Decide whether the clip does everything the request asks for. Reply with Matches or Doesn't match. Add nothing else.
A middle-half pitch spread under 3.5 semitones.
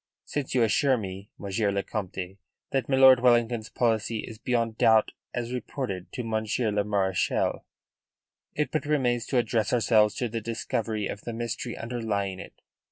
Matches